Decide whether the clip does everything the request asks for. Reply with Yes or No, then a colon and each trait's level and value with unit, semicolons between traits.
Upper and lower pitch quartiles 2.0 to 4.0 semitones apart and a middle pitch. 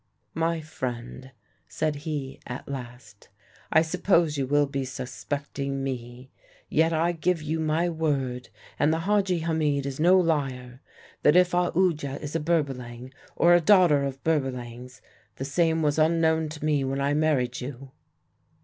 Yes: average, 3.4 semitones; medium, 145 Hz